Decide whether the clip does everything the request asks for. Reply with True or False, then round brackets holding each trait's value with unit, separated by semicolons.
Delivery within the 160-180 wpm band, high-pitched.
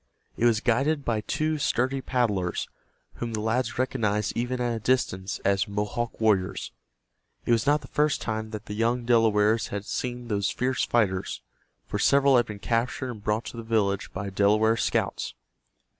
False (175 wpm; 115 Hz)